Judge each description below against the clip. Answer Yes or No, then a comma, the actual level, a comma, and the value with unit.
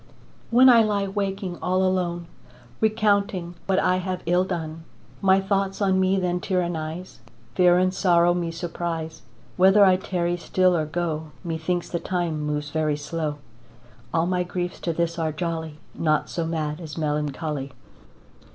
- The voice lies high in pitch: No, medium, 175 Hz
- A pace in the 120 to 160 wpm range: Yes, average, 150 wpm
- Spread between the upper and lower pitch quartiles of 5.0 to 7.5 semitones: No, narrow, 2.6 semitones